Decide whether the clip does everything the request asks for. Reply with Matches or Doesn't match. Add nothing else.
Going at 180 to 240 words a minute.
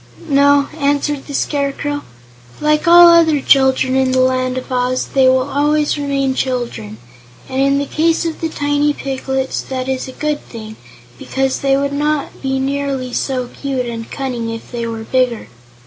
Doesn't match